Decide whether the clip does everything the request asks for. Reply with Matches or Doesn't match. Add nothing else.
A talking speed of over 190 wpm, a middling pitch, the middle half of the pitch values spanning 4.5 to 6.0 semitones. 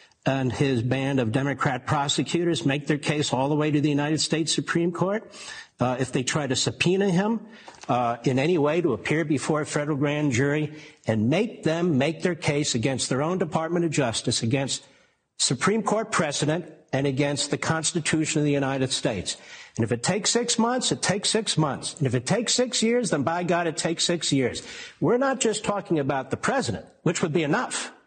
Doesn't match